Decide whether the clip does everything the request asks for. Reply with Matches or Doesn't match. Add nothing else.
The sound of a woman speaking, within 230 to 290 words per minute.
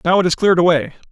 Doesn't match